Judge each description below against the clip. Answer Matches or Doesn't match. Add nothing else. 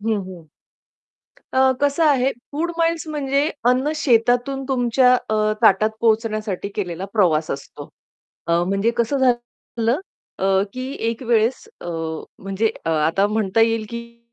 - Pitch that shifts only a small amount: Doesn't match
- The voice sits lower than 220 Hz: Doesn't match